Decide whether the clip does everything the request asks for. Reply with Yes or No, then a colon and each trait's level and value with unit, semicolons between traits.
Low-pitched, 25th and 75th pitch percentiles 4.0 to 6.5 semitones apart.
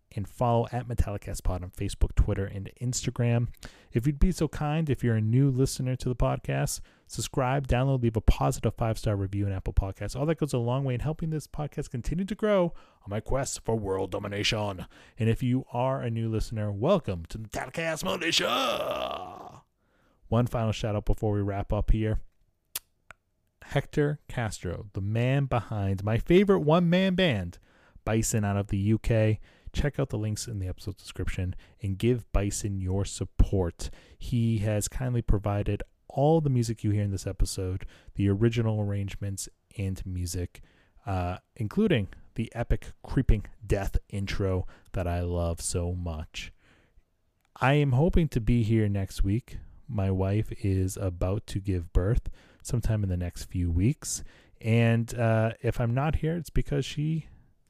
Yes: low, 110 Hz; average, 4.5 semitones